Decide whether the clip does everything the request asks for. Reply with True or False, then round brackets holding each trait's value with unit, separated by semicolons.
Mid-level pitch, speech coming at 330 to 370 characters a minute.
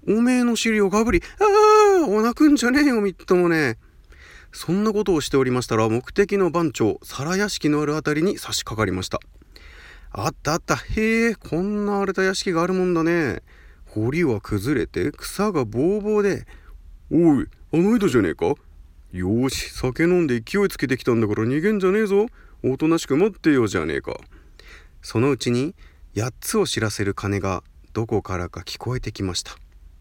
True (155 Hz; 345 characters per minute)